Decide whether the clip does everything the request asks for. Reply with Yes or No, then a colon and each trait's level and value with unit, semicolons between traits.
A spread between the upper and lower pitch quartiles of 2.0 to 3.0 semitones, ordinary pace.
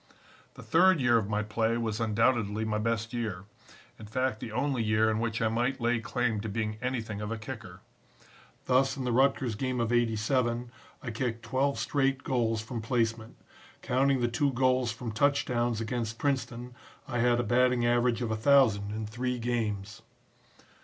Yes: narrow, 2.5 semitones; average, 175 wpm